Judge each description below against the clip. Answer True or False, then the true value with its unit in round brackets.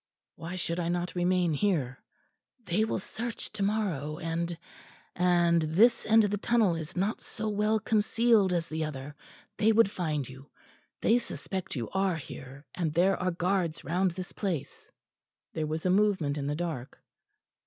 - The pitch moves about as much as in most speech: True (4.4 semitones)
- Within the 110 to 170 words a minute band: True (165 wpm)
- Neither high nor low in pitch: True (175 Hz)